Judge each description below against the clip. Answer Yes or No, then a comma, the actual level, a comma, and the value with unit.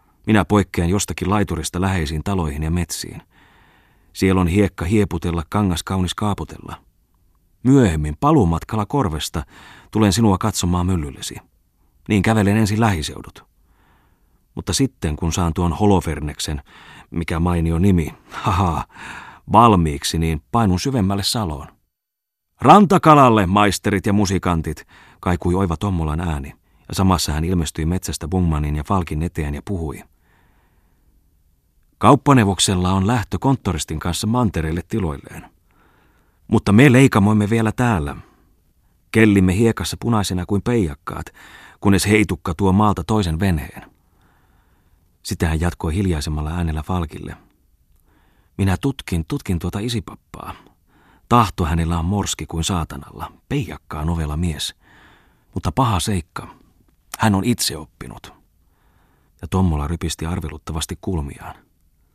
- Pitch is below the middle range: Yes, very low, 90 Hz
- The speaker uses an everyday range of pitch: Yes, average, 4.1 semitones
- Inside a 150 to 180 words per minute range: No, average, 110 wpm